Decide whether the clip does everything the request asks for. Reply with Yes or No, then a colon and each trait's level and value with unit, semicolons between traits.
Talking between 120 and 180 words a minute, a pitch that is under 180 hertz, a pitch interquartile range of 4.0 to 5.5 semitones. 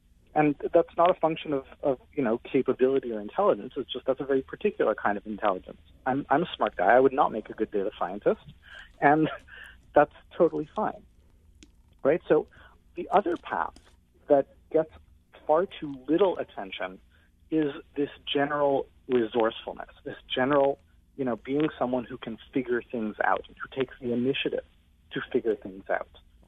Yes: average, 165 wpm; low, 135 Hz; average, 5.0 semitones